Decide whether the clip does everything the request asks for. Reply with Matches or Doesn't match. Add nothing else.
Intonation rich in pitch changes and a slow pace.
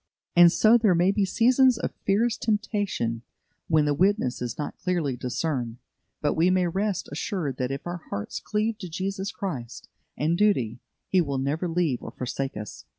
Doesn't match